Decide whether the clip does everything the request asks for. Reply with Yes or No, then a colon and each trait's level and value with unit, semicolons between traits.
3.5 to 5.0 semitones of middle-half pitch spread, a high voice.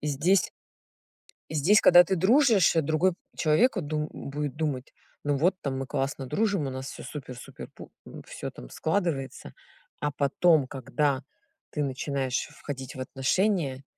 No: average, 4.7 semitones; medium, 150 Hz